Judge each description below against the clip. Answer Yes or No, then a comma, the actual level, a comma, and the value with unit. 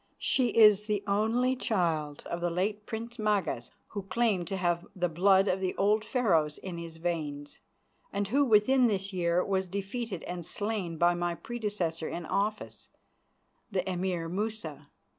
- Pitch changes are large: No, average, 3.7 semitones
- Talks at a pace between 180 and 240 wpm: No, average, 160 wpm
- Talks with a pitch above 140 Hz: Yes, high, 190 Hz